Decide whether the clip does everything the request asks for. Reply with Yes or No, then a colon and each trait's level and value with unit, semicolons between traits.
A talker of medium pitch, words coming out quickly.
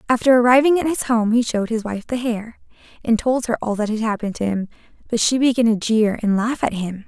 No: high, 230 Hz; fast, 245 wpm